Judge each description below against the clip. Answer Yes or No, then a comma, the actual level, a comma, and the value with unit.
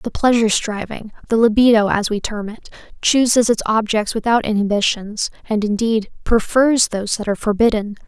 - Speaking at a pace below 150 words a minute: Yes, average, 140 wpm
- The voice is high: Yes, high, 220 Hz